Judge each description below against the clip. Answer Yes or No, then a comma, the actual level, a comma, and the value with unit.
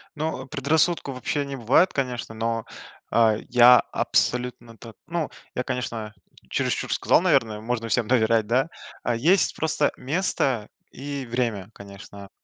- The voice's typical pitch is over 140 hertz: No, low, 125 Hz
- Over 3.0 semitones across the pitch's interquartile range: Yes, average, 3.6 semitones